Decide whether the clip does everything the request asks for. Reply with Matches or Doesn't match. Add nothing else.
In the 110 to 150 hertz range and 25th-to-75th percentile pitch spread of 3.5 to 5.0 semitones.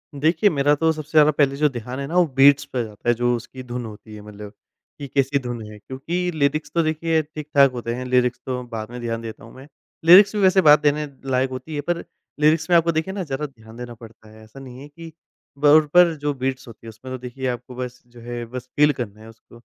Matches